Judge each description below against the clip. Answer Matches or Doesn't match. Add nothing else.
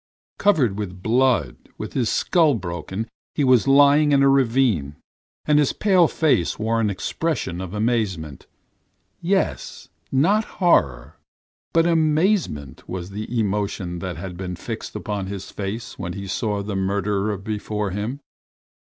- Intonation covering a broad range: Matches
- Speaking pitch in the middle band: Doesn't match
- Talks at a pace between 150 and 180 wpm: Doesn't match